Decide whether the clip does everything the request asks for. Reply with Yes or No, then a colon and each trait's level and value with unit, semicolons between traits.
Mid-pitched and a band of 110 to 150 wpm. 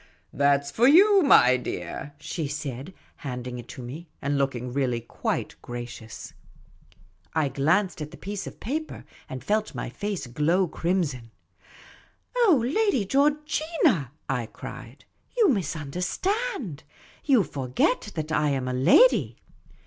Yes: medium, 155 Hz; average, 145 wpm